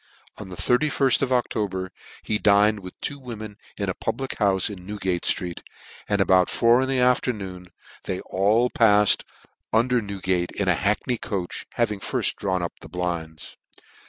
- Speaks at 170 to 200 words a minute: Yes, average, 175 wpm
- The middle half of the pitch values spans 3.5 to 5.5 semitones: Yes, average, 4.2 semitones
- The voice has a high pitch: No, low, 100 Hz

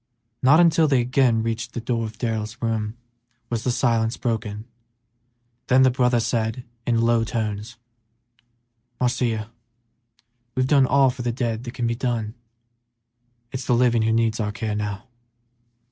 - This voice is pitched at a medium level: No, low, 115 Hz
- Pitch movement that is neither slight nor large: No, narrow, 2.1 semitones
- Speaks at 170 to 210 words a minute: No, average, 150 wpm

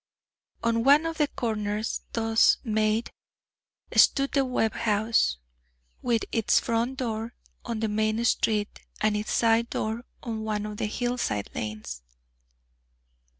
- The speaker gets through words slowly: Yes, slow, 130 wpm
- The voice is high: Yes, high, 225 Hz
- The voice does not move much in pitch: Yes, narrow, 1.8 semitones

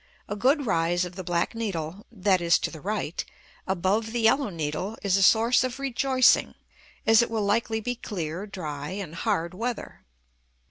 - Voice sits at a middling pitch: No, high, 200 Hz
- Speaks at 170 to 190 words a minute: Yes, average, 175 wpm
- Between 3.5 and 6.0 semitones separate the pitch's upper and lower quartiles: Yes, average, 4.7 semitones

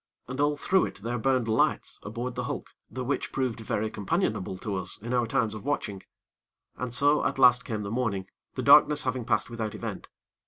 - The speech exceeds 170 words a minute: Yes, average, 200 wpm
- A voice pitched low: Yes, low, 120 Hz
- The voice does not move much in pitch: No, average, 3.5 semitones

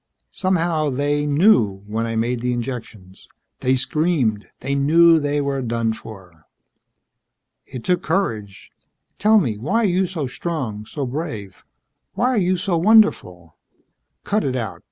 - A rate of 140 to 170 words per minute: Yes, average, 145 wpm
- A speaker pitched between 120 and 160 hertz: Yes, medium, 140 Hz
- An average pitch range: No, wide, 7.1 semitones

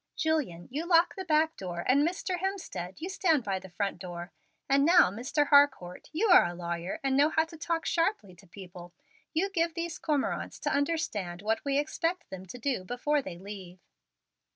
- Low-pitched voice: No, very high, 280 Hz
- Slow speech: No, average, 190 wpm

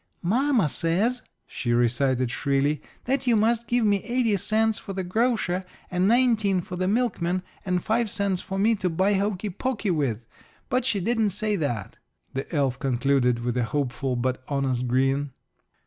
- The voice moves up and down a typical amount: No, wide, 8.2 semitones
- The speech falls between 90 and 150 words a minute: No, average, 165 wpm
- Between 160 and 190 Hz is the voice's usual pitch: Yes, medium, 185 Hz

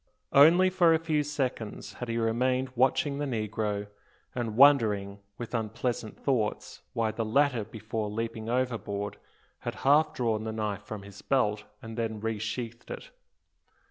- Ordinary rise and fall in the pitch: Yes, average, 3.5 semitones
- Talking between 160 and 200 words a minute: No, average, 145 wpm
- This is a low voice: Yes, low, 115 Hz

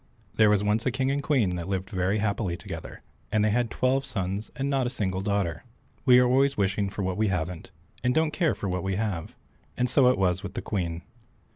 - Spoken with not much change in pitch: No, average, 5.0 semitones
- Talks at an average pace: No, fast, 230 wpm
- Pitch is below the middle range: Yes, low, 105 Hz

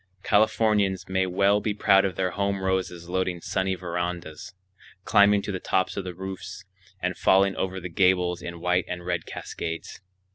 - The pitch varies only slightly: Yes, narrow, 1.6 semitones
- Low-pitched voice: Yes, very low, 95 Hz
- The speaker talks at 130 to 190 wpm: Yes, average, 170 wpm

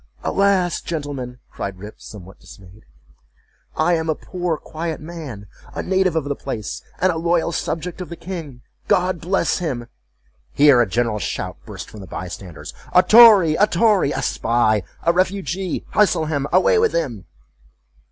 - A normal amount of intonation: No, wide, 7.3 semitones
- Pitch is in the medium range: Yes, medium, 160 Hz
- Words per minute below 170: Yes, average, 155 wpm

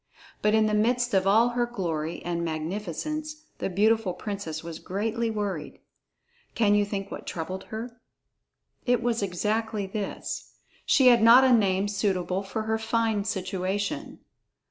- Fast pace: No, average, 145 wpm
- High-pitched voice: Yes, high, 210 Hz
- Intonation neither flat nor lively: Yes, average, 3.2 semitones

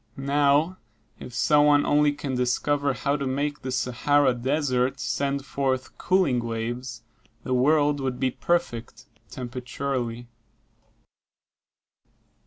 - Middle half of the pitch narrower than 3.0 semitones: Yes, narrow, 2.6 semitones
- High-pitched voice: No, low, 135 Hz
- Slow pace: Yes, slow, 110 wpm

